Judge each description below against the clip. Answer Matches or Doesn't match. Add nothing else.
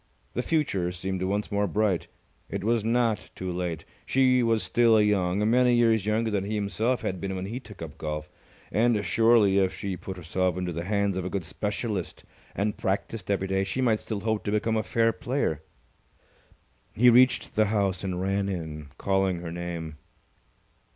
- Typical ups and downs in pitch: Matches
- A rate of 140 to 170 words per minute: Doesn't match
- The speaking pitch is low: Matches